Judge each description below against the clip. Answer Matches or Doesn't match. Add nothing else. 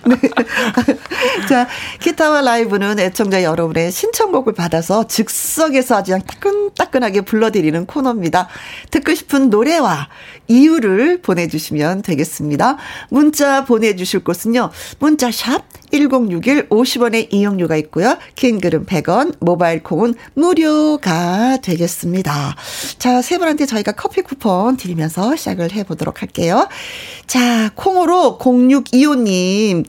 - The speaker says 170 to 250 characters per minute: Doesn't match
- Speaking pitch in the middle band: Doesn't match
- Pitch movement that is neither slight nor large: Doesn't match